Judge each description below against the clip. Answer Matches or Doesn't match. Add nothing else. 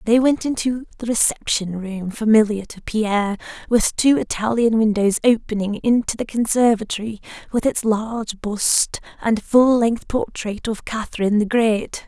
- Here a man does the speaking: Doesn't match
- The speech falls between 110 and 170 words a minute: Matches